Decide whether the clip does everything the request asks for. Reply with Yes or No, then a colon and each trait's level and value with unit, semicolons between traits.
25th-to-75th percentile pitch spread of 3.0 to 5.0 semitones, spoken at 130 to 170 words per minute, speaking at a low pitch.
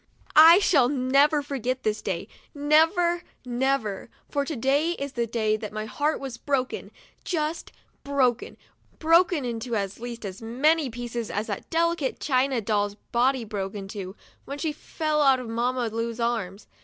No: average, 4.5 semitones; average, 160 wpm; very high, 255 Hz